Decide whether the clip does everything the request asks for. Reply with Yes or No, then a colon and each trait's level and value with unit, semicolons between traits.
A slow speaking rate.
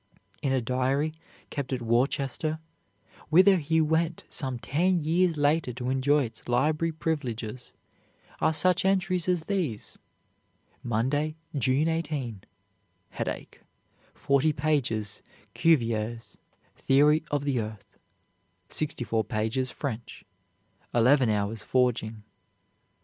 Yes: slow, 105 wpm